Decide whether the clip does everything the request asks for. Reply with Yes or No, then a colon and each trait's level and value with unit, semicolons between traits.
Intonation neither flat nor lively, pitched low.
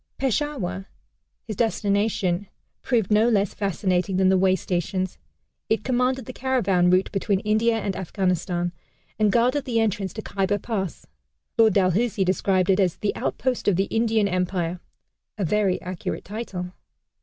No: average, 3.2 semitones; high, 200 Hz